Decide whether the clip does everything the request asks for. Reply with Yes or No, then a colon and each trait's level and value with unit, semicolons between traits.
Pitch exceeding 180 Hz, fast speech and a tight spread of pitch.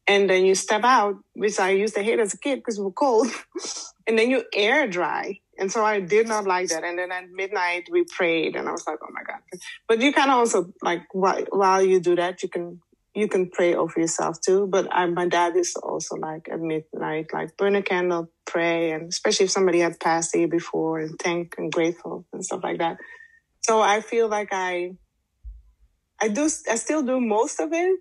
No: high, 190 Hz; fast, 225 wpm; average, 4.0 semitones